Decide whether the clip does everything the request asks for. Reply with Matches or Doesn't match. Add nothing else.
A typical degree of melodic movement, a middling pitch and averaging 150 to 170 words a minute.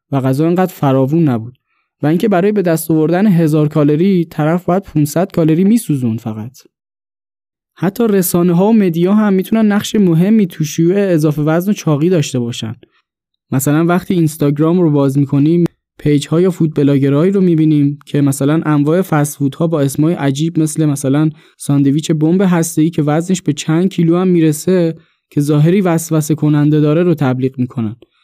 Matches